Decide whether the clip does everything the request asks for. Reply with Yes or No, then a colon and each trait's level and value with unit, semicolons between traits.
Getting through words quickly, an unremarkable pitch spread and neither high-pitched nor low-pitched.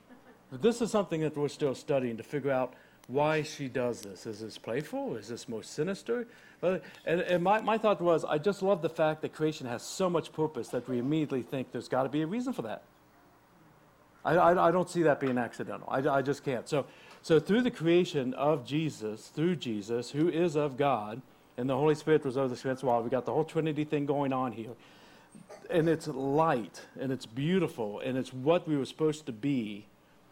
Yes: fast, 210 wpm; average, 4.5 semitones; medium, 150 Hz